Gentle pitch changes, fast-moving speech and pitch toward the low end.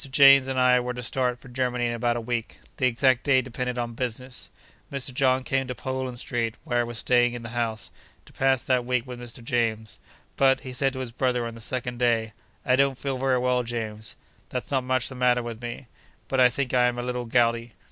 Yes: narrow, 1.5 semitones; fast, 230 wpm; low, 125 Hz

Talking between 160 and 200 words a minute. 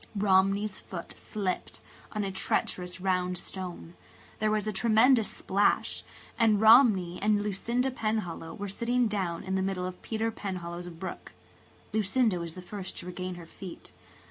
No: average, 145 wpm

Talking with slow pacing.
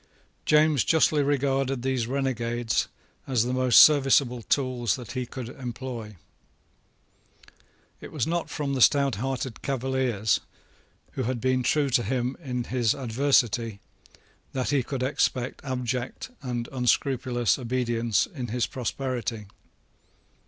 Yes: slow, 120 wpm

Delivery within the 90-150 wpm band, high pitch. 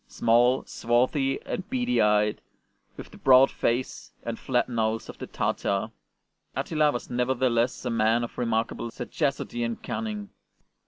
No: average, 140 wpm; low, 120 Hz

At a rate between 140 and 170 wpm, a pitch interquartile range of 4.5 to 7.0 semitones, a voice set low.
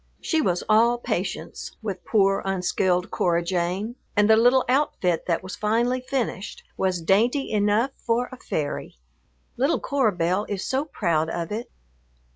No: average, 150 wpm; average, 5.0 semitones; high, 210 Hz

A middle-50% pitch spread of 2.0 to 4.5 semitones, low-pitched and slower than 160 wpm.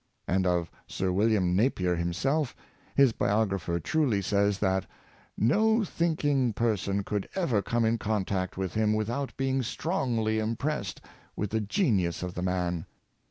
No: wide, 5.6 semitones; low, 105 Hz; average, 145 wpm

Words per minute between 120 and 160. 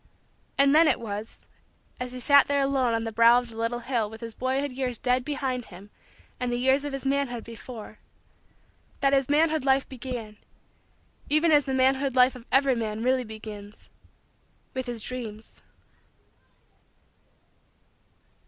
Yes: average, 155 wpm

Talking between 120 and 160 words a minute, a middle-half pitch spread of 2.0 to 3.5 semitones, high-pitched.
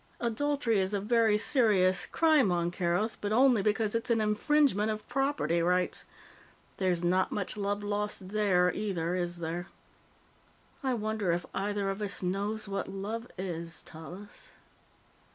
Yes: average, 145 wpm; average, 3.2 semitones; high, 205 Hz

